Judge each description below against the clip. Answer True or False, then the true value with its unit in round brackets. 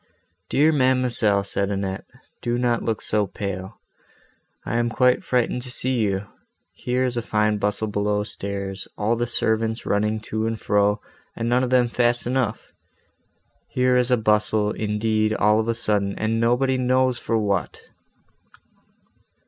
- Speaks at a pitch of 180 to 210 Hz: False (110 Hz)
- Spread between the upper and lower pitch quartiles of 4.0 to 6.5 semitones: False (2.9 semitones)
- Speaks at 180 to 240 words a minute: False (155 wpm)